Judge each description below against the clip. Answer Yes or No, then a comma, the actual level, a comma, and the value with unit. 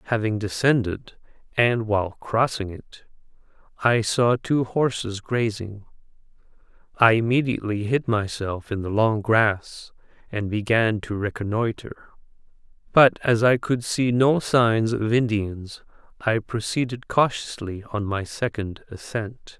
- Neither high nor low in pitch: No, low, 110 Hz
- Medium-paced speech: No, slow, 120 wpm